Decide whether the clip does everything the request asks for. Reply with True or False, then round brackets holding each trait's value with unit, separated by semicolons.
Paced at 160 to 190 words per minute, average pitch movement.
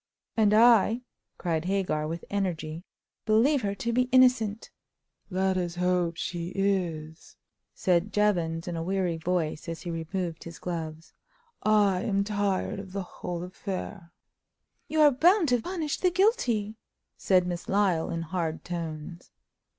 False (145 wpm; 4.0 semitones)